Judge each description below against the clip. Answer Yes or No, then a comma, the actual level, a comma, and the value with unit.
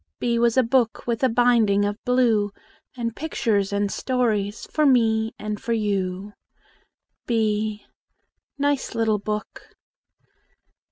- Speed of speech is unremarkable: No, slow, 120 wpm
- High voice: Yes, high, 225 Hz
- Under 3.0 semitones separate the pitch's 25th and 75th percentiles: Yes, narrow, 2.6 semitones